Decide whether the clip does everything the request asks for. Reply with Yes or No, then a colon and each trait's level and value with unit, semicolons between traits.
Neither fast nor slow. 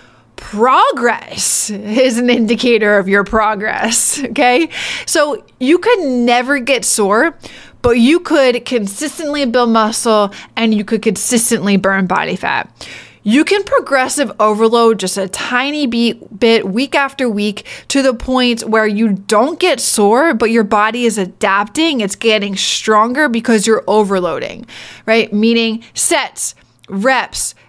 No: slow, 130 wpm